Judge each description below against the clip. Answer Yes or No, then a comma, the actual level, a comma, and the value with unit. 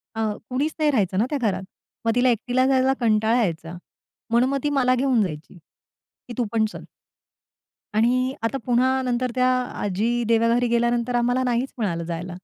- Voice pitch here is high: Yes, high, 240 Hz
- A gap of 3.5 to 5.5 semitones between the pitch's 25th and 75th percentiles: No, average, 2.7 semitones